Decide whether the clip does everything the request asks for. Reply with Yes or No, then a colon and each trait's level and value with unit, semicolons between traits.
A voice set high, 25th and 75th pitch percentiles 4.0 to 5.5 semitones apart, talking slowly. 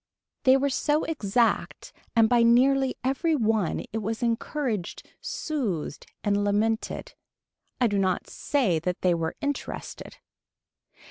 Yes: high, 230 Hz; average, 5.0 semitones; slow, 125 wpm